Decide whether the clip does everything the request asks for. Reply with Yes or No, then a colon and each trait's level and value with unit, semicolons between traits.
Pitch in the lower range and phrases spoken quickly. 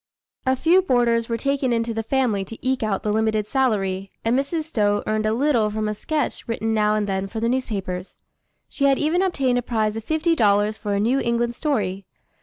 No: high, 230 Hz; fast, 210 wpm